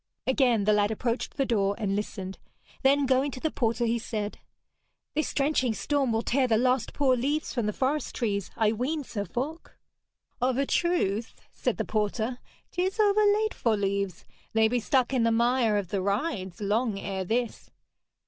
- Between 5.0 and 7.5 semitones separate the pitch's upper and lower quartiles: No, average, 4.5 semitones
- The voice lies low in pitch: No, high, 235 Hz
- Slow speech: No, average, 175 wpm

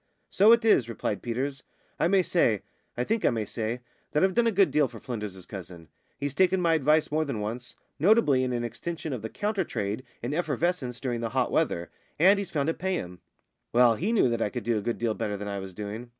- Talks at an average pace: No, fast, 235 wpm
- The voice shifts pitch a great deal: Yes, wide, 7.3 semitones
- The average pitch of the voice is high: No, low, 125 Hz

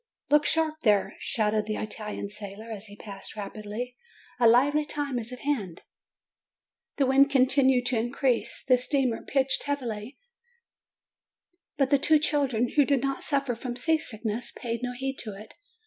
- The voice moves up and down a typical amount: Yes, average, 4.1 semitones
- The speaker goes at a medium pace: Yes, average, 155 wpm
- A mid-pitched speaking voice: No, very high, 250 Hz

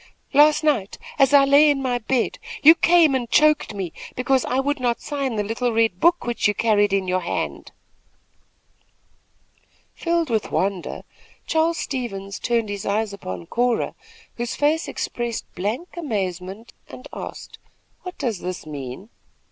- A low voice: No, high, 240 Hz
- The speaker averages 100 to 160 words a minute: Yes, average, 150 wpm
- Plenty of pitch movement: Yes, wide, 6.1 semitones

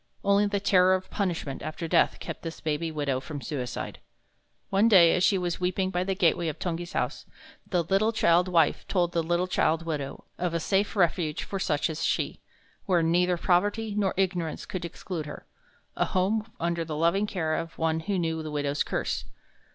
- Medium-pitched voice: Yes, medium, 175 Hz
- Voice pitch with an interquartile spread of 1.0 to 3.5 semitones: Yes, average, 2.8 semitones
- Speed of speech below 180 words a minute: No, average, 190 wpm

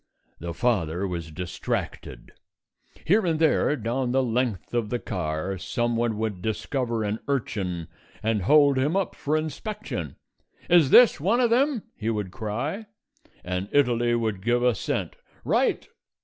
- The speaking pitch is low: Yes, low, 120 Hz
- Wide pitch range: Yes, wide, 6.5 semitones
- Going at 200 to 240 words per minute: No, average, 140 wpm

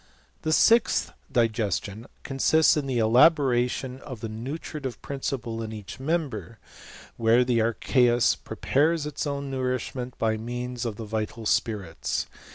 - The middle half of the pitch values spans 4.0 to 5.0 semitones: No, average, 3.5 semitones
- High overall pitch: No, low, 125 Hz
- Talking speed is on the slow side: Yes, slow, 125 wpm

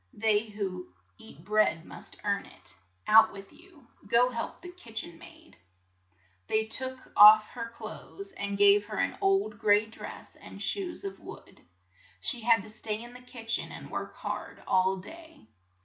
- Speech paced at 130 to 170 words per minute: No, average, 180 wpm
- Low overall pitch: No, high, 220 Hz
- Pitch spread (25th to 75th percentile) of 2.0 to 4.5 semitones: Yes, average, 3.6 semitones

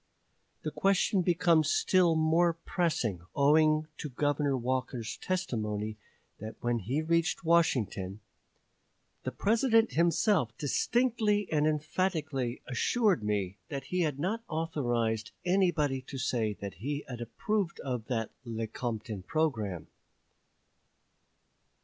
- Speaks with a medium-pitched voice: Yes, medium, 145 Hz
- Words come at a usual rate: No, slow, 110 wpm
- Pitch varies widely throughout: Yes, wide, 6.7 semitones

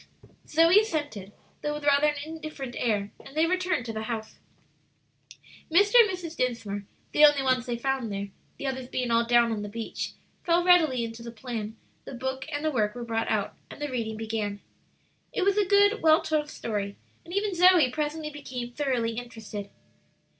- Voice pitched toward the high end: Yes, very high, 260 Hz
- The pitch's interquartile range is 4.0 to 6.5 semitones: Yes, wide, 5.6 semitones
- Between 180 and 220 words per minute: Yes, average, 185 wpm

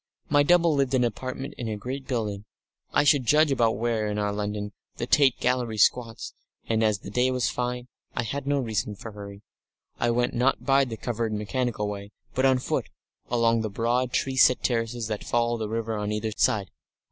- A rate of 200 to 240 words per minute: Yes, fast, 205 wpm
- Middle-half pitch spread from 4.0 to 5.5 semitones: No, average, 3.2 semitones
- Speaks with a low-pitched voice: Yes, low, 120 Hz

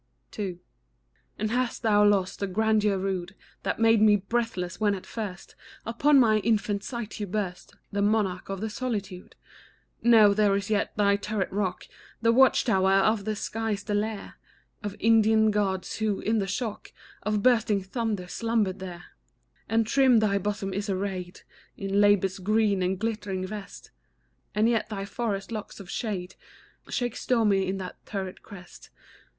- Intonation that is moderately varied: No, narrow, 2.3 semitones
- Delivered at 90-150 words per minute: No, average, 160 wpm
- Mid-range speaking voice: No, high, 205 Hz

